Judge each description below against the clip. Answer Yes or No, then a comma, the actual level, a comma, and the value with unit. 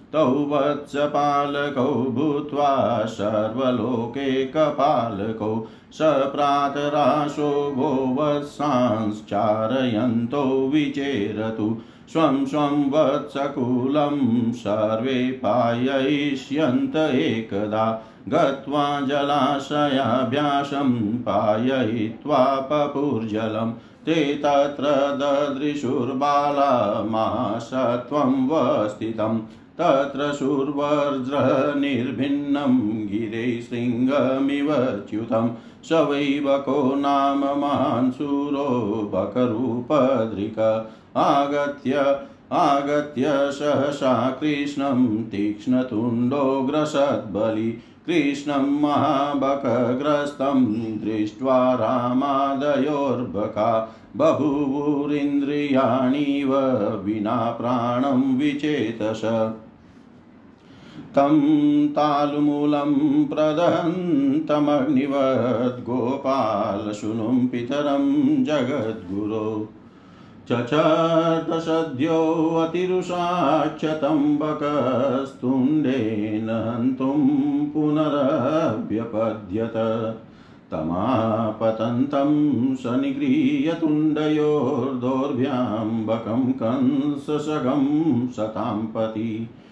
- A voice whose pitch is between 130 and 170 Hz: Yes, medium, 140 Hz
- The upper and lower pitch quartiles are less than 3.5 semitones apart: No, average, 4.1 semitones